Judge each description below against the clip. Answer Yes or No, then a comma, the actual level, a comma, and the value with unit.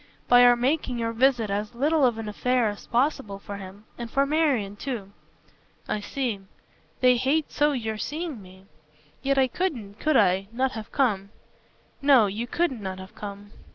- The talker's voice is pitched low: No, high, 235 Hz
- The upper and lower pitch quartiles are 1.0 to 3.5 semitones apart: No, average, 4.9 semitones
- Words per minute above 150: Yes, average, 175 wpm